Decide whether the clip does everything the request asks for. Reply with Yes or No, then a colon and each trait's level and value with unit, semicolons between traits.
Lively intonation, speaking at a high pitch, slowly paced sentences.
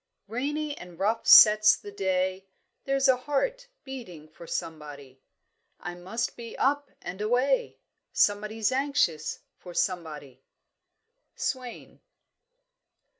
Yes: wide, 7.1 semitones; high, 210 Hz; slow, 105 wpm